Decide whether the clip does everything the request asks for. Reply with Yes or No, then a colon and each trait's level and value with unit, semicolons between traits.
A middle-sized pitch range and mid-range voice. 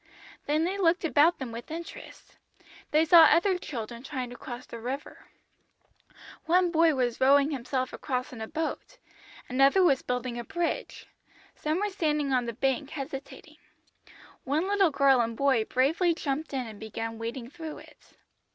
No: average, 4.6 semitones; very high, 275 Hz